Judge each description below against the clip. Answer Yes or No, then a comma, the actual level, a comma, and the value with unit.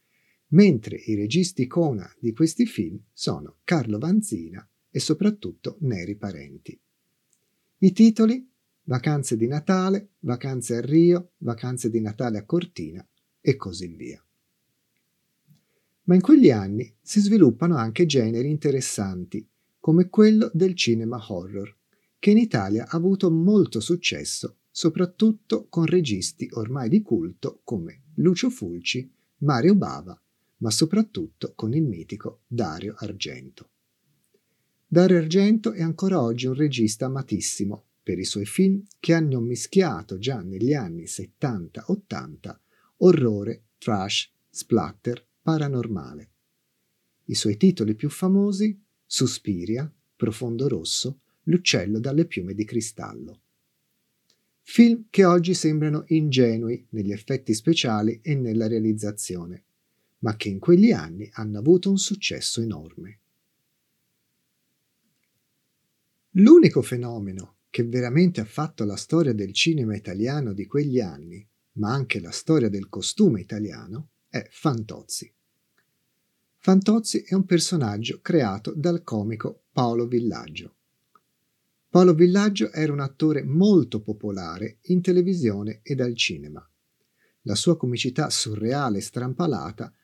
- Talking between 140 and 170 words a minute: No, slow, 115 wpm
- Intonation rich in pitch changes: Yes, wide, 8.1 semitones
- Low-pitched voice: Yes, low, 130 Hz